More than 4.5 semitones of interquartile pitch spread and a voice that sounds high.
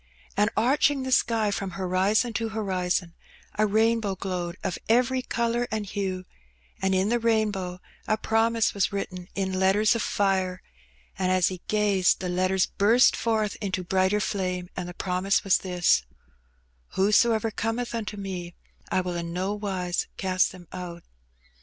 No: average, 3.1 semitones; high, 195 Hz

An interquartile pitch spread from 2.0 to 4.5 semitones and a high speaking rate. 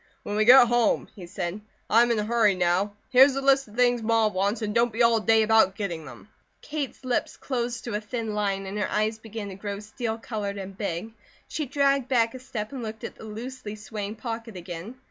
Yes: average, 2.8 semitones; fast, 225 wpm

